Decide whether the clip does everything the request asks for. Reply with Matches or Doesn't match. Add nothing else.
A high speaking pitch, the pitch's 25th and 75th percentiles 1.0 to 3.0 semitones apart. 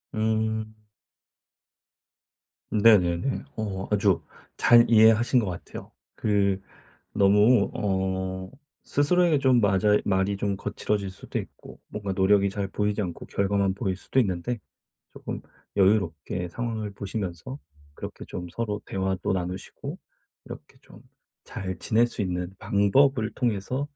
Doesn't match